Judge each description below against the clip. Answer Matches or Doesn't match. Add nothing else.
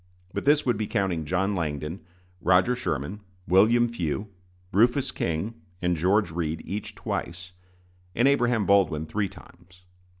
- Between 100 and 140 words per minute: Matches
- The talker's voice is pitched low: Matches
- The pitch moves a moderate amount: Matches